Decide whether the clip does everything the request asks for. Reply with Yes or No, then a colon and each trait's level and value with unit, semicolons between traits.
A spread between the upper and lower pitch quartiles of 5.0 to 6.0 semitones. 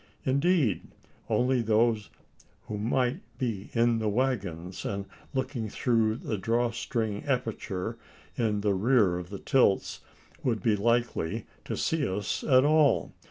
No: average, 3.8 semitones